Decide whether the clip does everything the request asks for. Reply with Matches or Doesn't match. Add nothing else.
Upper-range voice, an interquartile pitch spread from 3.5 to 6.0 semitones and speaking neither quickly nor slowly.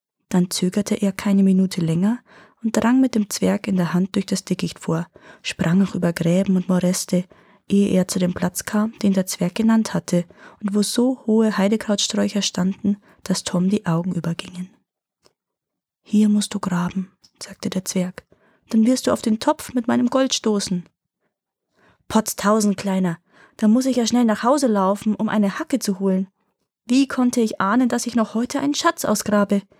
Doesn't match